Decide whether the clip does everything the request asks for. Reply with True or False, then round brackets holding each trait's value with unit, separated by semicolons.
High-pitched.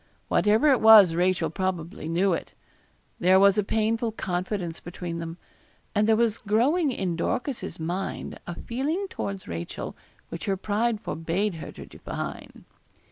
True (195 Hz)